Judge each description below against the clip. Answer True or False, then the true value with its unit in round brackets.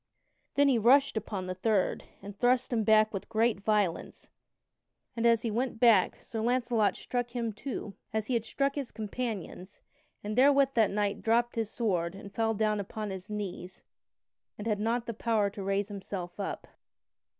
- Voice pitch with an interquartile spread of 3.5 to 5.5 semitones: False (2.8 semitones)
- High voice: True (220 Hz)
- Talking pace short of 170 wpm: False (175 wpm)